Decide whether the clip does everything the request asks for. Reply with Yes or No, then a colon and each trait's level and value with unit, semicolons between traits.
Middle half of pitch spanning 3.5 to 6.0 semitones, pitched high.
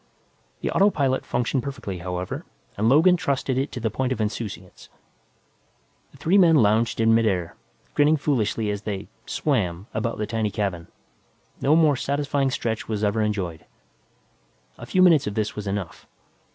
No: average, 5.3 semitones; low, 115 Hz